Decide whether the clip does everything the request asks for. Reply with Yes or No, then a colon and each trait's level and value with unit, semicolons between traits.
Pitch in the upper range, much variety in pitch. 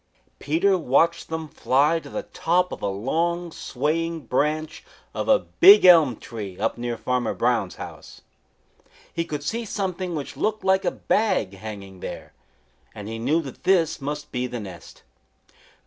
No: medium, 150 Hz; wide, 6.2 semitones